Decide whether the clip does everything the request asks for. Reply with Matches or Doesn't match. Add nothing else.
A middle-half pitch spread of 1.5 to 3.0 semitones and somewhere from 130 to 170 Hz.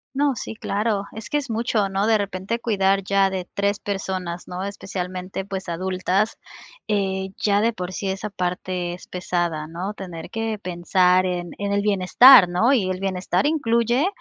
Doesn't match